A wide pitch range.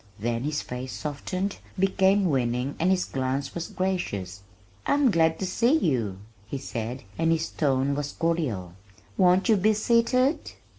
Yes: wide, 6.7 semitones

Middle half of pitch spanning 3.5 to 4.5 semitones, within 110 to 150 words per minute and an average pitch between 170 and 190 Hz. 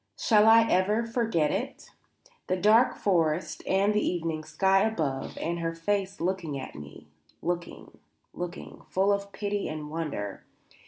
Yes: average, 4.2 semitones; average, 145 wpm; medium, 185 Hz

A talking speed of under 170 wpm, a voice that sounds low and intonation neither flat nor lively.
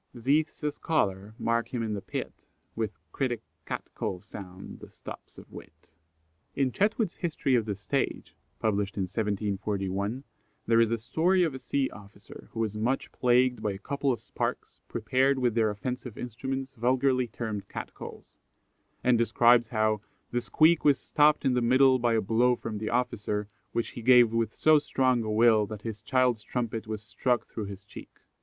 No: average, 175 wpm; low, 115 Hz; average, 3.3 semitones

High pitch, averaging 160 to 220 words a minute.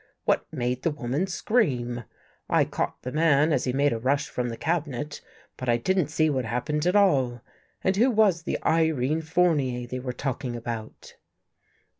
No: medium, 140 Hz; average, 175 wpm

